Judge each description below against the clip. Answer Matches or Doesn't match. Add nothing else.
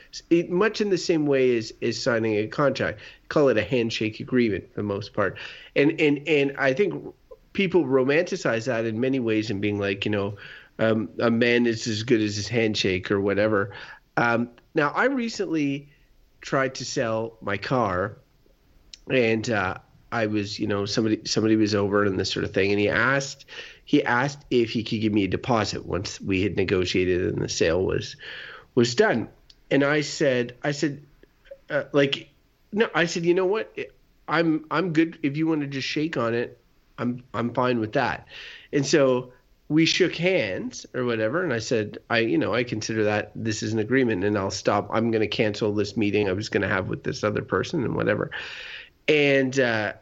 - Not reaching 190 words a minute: Doesn't match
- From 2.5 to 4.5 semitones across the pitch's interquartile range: Doesn't match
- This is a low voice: Matches